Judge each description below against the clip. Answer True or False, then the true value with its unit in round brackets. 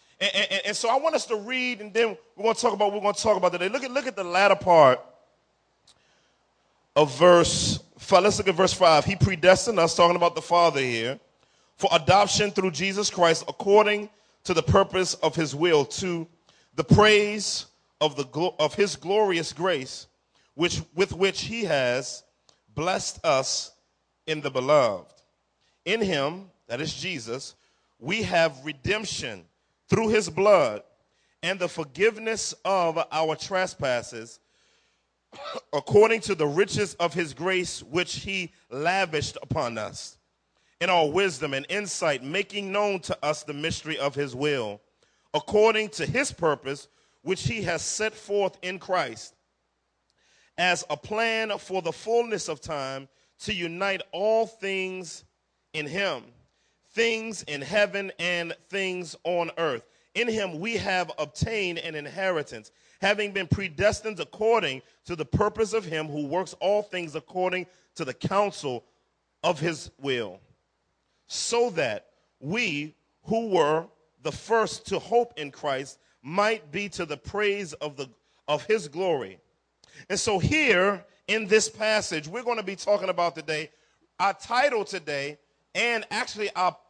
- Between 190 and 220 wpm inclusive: False (150 wpm)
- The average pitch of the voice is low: False (185 Hz)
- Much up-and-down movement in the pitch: False (4.9 semitones)